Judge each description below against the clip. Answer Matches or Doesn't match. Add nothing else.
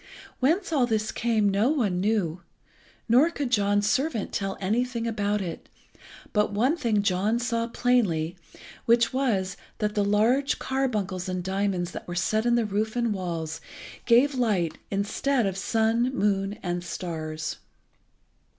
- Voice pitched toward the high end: Matches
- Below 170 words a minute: Matches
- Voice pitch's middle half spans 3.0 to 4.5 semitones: Matches